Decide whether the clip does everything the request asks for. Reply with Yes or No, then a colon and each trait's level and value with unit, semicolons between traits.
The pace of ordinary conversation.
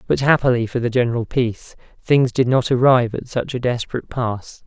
Yes: average, 195 wpm